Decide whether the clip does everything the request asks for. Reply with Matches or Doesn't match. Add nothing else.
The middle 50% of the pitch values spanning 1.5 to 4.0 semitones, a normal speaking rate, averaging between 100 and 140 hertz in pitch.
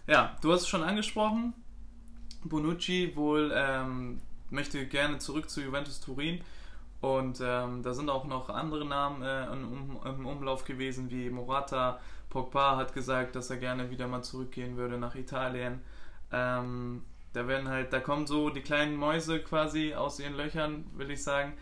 Matches